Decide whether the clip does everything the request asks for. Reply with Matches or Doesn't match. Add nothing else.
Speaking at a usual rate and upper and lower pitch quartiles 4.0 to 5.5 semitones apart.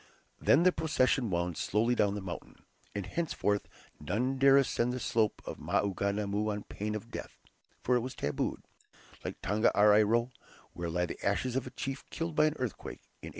Matches